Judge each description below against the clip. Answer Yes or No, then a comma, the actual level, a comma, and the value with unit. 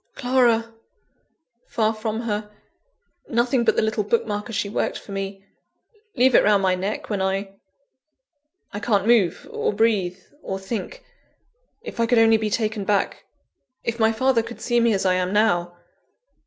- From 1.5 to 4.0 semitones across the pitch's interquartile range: Yes, average, 2.8 semitones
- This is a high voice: Yes, high, 215 Hz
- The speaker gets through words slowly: No, average, 165 wpm